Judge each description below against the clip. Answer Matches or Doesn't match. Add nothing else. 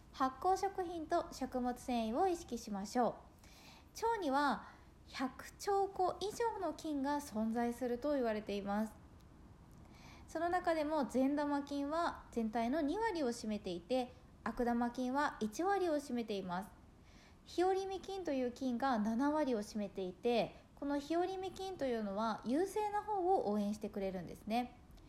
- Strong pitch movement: Matches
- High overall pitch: Matches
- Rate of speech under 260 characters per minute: Doesn't match